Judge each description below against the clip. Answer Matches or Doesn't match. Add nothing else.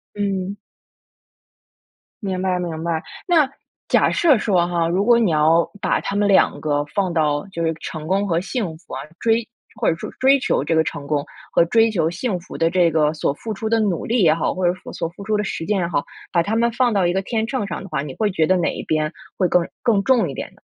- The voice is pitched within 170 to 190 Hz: Matches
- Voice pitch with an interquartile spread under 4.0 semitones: Doesn't match